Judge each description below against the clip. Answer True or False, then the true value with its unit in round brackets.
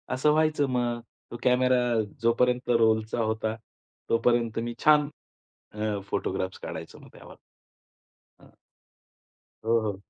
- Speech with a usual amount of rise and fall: False (2.3 semitones)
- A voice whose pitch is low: True (120 Hz)